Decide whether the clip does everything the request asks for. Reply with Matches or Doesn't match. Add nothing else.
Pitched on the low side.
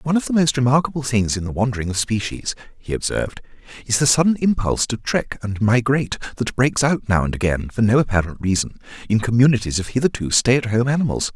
Matches